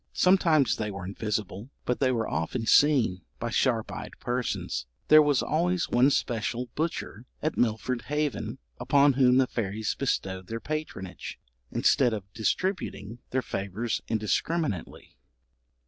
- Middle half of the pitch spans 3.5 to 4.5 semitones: No, average, 5.1 semitones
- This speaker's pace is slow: Yes, slow, 130 wpm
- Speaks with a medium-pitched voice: No, low, 120 Hz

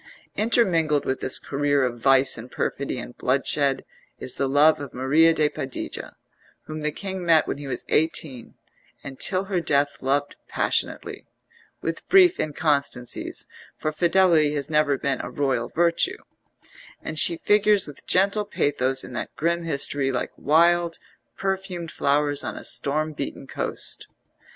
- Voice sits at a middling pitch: Yes, medium, 150 Hz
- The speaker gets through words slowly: No, average, 150 wpm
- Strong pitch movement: No, average, 3.7 semitones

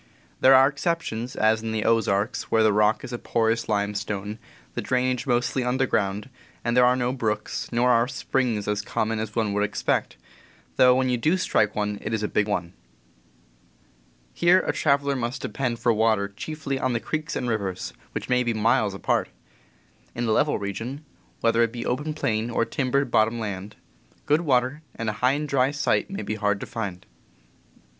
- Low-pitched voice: Yes, low, 115 Hz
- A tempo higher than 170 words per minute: Yes, average, 190 wpm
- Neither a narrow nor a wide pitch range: Yes, average, 3.3 semitones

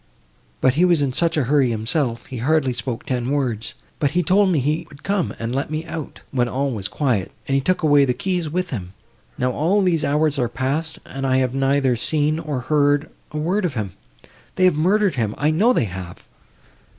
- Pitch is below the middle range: No, medium, 145 Hz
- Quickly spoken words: Yes, fast, 210 wpm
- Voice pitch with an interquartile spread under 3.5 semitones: No, average, 4.1 semitones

